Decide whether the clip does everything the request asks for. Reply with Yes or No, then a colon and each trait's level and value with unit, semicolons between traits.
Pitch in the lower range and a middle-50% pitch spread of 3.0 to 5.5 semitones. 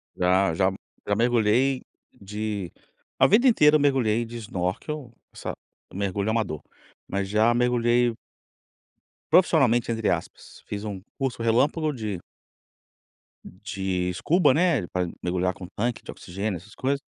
Yes: low, 110 Hz; average, 4.9 semitones